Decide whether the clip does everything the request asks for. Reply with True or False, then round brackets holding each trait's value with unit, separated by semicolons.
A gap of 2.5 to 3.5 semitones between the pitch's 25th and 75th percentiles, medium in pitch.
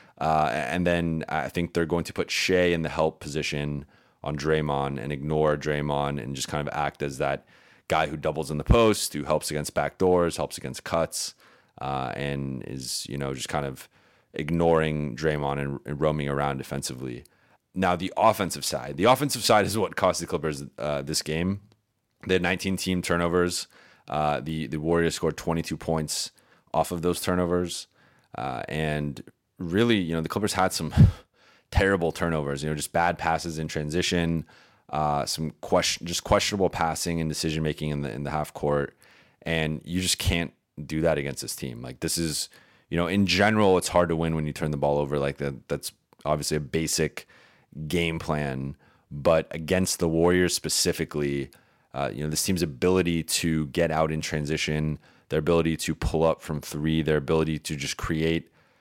False (2.8 semitones; 80 Hz)